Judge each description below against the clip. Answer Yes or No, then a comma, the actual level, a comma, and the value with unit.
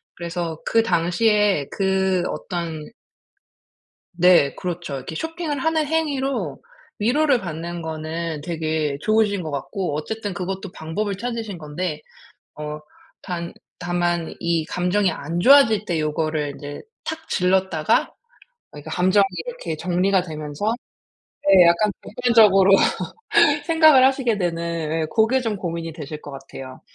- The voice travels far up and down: No, average, 4.9 semitones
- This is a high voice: No, medium, 180 Hz